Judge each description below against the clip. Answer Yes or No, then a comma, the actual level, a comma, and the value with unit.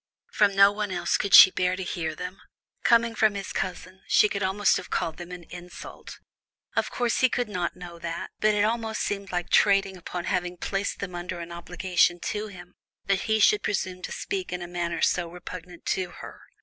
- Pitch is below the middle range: No, medium, 185 Hz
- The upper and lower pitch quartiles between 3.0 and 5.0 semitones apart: No, narrow, 2.5 semitones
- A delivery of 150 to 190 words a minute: No, fast, 205 wpm